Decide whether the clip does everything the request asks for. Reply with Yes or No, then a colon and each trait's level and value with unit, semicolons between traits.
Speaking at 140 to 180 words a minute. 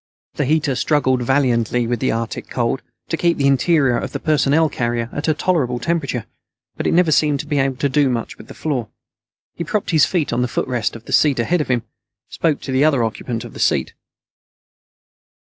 No: average, 200 wpm